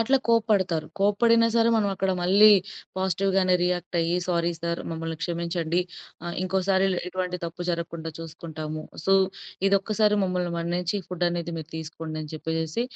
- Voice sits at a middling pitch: Yes, medium, 180 Hz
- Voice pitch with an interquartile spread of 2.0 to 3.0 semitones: Yes, average, 2.7 semitones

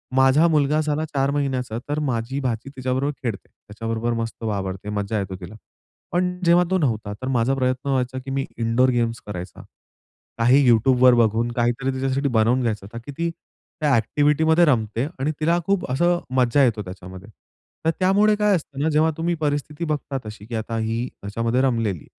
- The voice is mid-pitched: No, low, 130 Hz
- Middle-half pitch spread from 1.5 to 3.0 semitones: No, average, 4.4 semitones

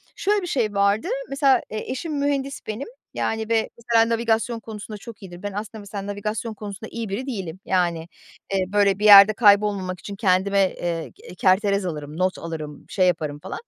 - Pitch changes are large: No, average, 3.3 semitones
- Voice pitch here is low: No, high, 205 Hz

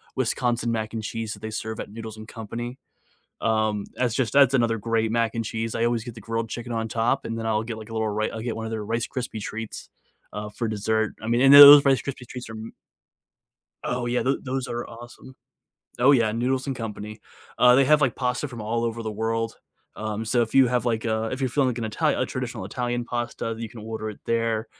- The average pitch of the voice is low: Yes, low, 115 Hz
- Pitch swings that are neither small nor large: No, narrow, 1.8 semitones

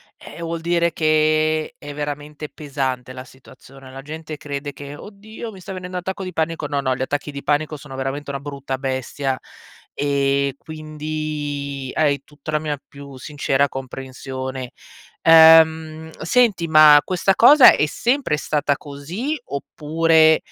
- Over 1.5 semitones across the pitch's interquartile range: Yes, narrow, 2.4 semitones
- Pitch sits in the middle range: Yes, medium, 150 Hz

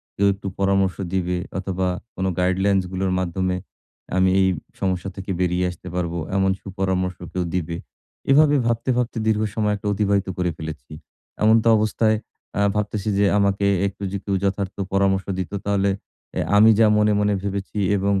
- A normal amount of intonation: No, narrow, 1.9 semitones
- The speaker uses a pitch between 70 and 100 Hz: Yes, very low, 95 Hz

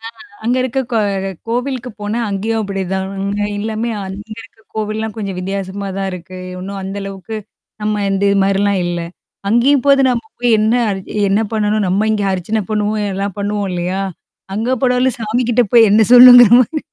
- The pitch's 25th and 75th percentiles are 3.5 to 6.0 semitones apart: No, average, 2.7 semitones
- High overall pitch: Yes, high, 210 Hz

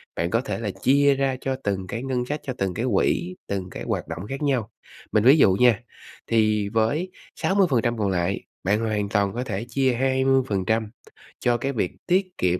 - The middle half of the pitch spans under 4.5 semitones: No, average, 4.8 semitones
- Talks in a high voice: No, low, 115 Hz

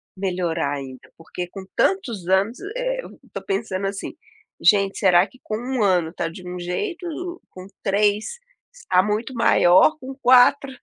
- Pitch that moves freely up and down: Yes, wide, 6.2 semitones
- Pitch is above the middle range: Yes, high, 200 Hz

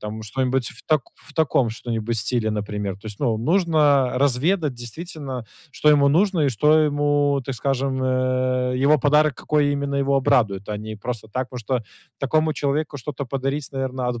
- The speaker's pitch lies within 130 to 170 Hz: Yes, low, 135 Hz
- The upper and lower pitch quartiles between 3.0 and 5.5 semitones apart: Yes, average, 3.4 semitones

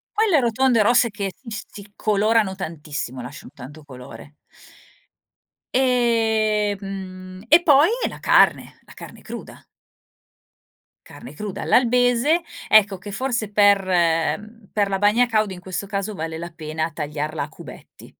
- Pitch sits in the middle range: No, high, 205 Hz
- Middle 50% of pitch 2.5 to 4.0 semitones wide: No, average, 4.7 semitones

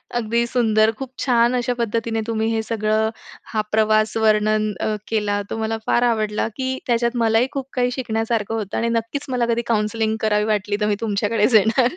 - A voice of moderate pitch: No, high, 225 Hz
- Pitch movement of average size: No, narrow, 1.6 semitones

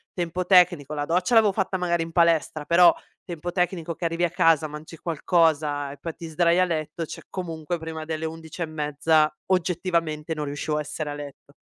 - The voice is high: No, medium, 165 Hz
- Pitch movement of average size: No, narrow, 2.3 semitones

